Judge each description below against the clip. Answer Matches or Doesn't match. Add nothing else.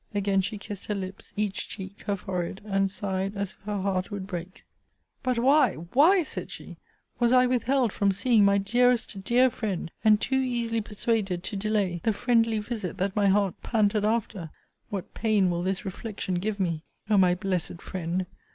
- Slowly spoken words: Doesn't match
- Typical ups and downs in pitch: Matches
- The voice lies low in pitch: Doesn't match